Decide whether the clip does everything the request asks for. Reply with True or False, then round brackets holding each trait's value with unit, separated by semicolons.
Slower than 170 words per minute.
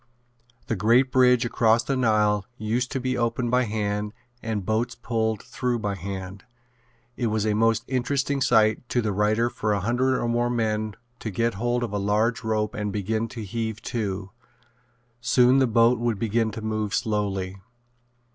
False (175 wpm)